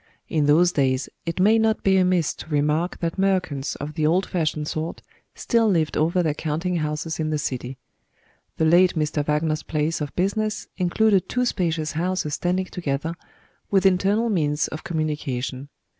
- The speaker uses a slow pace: No, average, 165 wpm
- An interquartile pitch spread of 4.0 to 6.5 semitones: No, average, 3.5 semitones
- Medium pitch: Yes, medium, 160 Hz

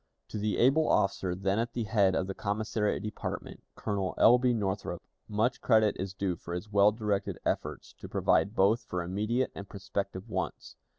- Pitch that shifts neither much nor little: No, narrow, 2.3 semitones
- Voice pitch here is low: Yes, low, 105 Hz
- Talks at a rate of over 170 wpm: Yes, average, 180 wpm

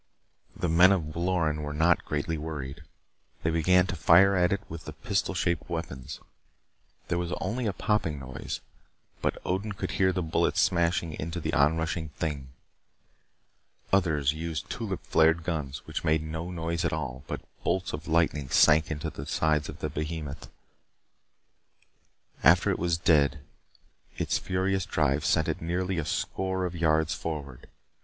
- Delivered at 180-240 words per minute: No, average, 160 wpm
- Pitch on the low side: Yes, very low, 80 Hz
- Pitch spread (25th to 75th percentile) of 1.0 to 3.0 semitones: Yes, average, 2.7 semitones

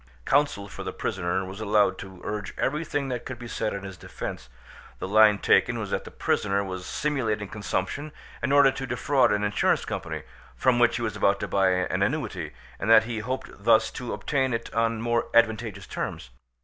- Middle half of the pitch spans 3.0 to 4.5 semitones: Yes, average, 3.8 semitones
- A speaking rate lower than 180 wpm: No, average, 195 wpm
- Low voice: Yes, low, 110 Hz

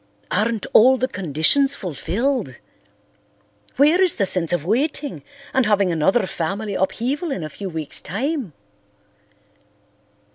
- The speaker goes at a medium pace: No, slow, 120 wpm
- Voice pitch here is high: Yes, high, 210 Hz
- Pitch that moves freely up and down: Yes, wide, 7.0 semitones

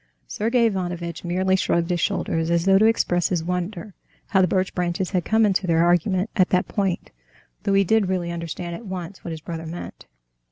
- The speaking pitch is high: No, medium, 180 Hz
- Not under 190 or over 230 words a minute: Yes, average, 200 wpm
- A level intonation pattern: Yes, narrow, 2.2 semitones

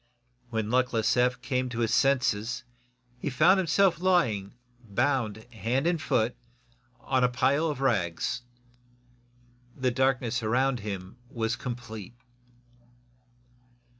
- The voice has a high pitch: No, low, 125 Hz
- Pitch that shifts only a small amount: No, average, 3.4 semitones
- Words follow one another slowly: Yes, slow, 110 wpm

